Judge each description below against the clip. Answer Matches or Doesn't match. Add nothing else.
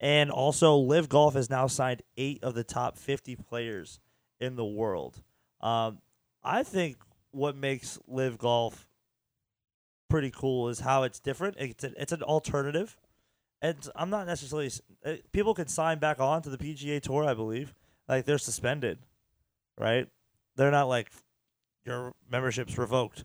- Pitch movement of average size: Matches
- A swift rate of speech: Doesn't match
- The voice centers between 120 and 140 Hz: Matches